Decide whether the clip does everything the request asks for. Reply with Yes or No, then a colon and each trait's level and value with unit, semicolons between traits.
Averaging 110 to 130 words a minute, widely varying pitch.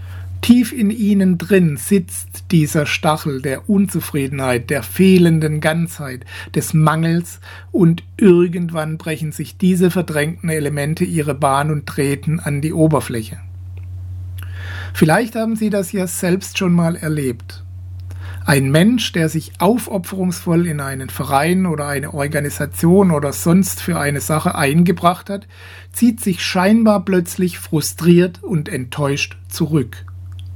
Yes: slow, 125 wpm; wide, 5.8 semitones